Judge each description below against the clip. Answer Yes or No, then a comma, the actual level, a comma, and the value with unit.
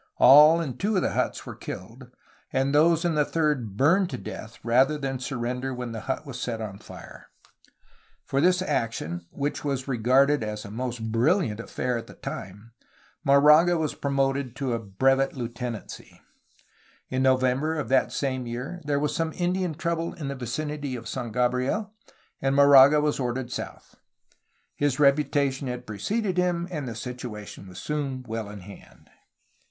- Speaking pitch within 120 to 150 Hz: Yes, low, 135 Hz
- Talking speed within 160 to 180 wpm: Yes, average, 165 wpm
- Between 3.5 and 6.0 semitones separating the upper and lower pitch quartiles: Yes, average, 3.8 semitones